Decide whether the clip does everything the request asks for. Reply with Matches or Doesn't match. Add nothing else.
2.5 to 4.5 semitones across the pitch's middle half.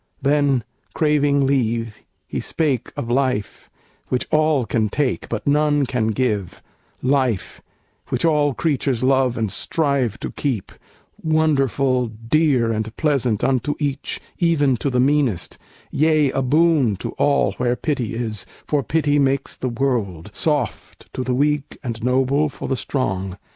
Matches